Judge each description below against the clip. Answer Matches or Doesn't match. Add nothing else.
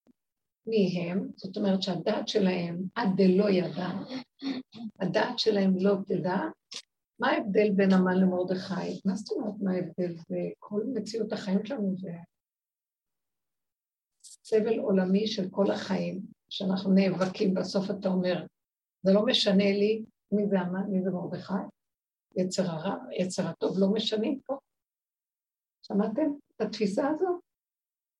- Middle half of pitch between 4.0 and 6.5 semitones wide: Doesn't match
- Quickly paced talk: Doesn't match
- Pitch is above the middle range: Matches